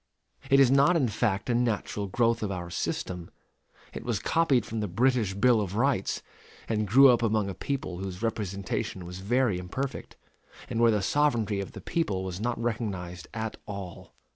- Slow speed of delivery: No, average, 185 wpm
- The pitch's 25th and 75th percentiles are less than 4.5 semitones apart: Yes, average, 4.1 semitones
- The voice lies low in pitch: Yes, low, 110 Hz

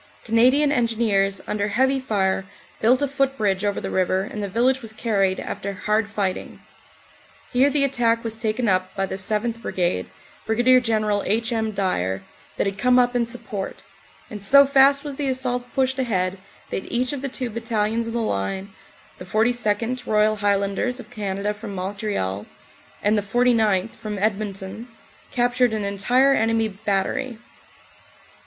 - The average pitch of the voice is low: No, high, 220 Hz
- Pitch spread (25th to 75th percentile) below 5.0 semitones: Yes, average, 3.8 semitones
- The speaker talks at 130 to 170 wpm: Yes, average, 160 wpm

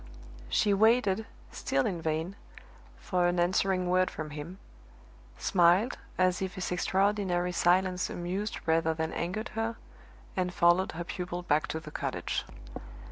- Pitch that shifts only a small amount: Yes, narrow, 1.9 semitones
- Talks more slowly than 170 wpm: Yes, slow, 135 wpm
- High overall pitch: No, medium, 180 Hz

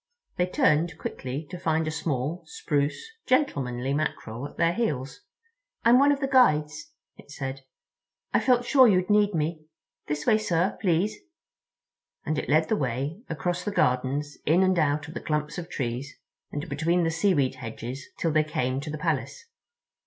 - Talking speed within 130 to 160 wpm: No, average, 170 wpm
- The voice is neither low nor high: Yes, medium, 155 Hz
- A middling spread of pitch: Yes, average, 4.4 semitones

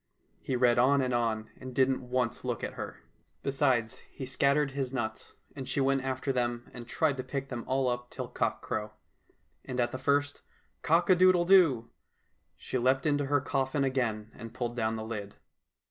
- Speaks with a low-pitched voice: Yes, low, 130 Hz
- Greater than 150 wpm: Yes, average, 190 wpm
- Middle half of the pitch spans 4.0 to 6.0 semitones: No, narrow, 2.4 semitones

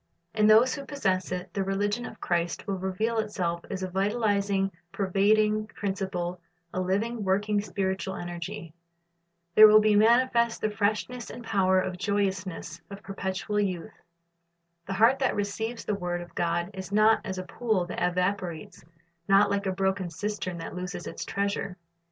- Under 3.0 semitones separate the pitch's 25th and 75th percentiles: Yes, narrow, 2.4 semitones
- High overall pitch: Yes, high, 195 Hz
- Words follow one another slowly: No, average, 160 wpm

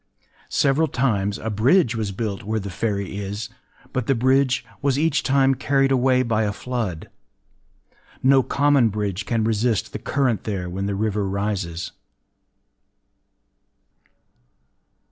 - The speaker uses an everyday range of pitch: Yes, average, 4.8 semitones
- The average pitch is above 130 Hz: No, low, 110 Hz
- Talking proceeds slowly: Yes, slow, 130 wpm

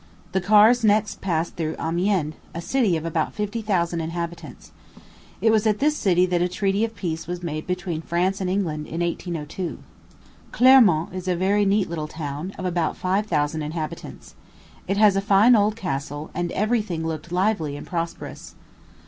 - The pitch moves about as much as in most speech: Yes, average, 3.8 semitones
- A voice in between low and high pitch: Yes, medium, 180 Hz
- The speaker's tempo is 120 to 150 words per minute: No, average, 175 wpm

